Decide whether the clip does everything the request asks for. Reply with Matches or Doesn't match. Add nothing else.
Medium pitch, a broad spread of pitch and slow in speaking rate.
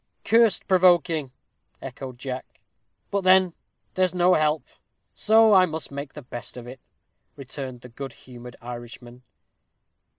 Matches